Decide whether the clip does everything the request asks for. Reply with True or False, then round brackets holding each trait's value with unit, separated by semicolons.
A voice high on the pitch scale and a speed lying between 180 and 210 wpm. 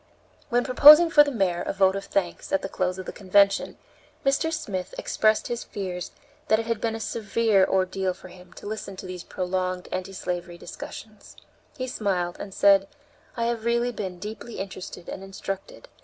True (195 Hz; 185 wpm)